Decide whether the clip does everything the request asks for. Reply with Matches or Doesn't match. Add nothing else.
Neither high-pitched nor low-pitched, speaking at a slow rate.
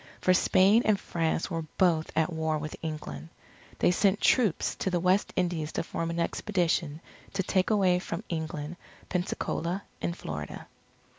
Doesn't match